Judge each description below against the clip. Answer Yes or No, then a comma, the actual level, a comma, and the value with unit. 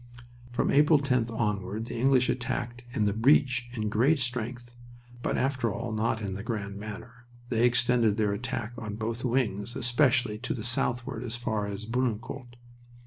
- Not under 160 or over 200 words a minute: Yes, average, 165 wpm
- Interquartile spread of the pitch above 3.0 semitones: No, narrow, 2.5 semitones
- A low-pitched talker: Yes, low, 120 Hz